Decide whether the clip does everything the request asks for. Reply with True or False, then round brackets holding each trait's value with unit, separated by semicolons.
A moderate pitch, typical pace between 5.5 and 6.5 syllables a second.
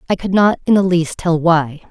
False (175 Hz; 5.0 syllables/s)